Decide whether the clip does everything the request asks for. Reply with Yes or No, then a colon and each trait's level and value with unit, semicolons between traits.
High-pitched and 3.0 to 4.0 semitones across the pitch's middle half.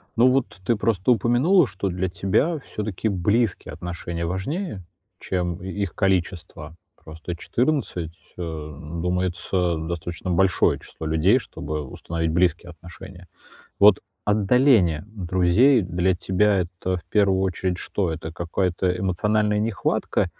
No: very low, 95 Hz; average, 3.3 semitones